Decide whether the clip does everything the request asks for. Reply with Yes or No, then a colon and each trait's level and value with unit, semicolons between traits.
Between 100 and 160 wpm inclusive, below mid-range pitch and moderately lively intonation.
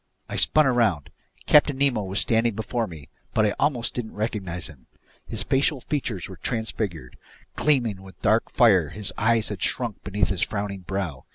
No: average, 170 wpm; low, 105 Hz; average, 3.9 semitones